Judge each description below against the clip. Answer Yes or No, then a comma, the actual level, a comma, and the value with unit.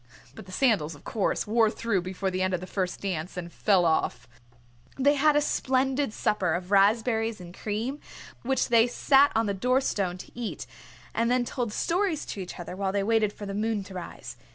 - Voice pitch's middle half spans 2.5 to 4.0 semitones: No, average, 4.8 semitones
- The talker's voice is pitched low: No, high, 210 Hz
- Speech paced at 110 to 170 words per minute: No, fast, 205 wpm